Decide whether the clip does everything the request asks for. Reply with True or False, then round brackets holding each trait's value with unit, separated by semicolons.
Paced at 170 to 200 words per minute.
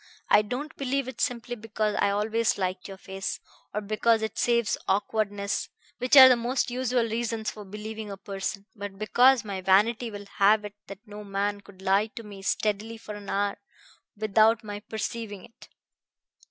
True (175 wpm)